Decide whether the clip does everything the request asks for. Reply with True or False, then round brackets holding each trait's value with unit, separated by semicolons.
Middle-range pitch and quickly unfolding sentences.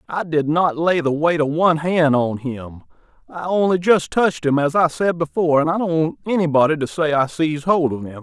True (155 Hz; 235 wpm)